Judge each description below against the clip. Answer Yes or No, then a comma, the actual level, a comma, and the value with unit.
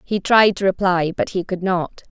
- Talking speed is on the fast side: Yes, fast, 220 wpm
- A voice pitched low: No, medium, 185 Hz